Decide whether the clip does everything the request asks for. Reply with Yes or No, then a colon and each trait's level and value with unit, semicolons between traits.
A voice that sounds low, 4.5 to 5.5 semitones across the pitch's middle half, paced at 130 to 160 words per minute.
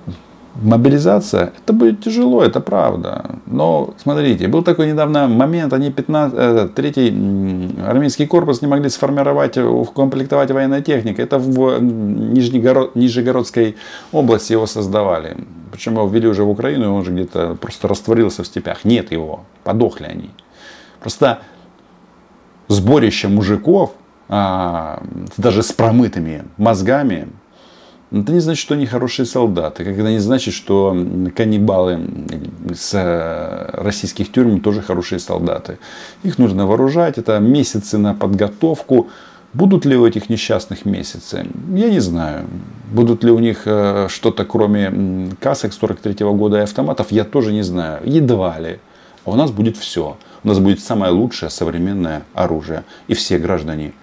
Yes: low, 110 Hz; average, 5.2 semitones; average, 135 wpm